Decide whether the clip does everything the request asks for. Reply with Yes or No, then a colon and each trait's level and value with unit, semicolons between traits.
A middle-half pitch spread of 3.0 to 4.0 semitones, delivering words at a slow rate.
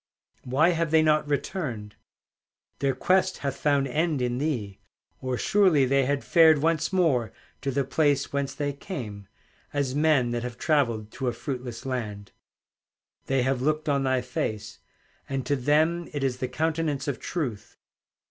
No: average, 3.7 semitones; average, 160 wpm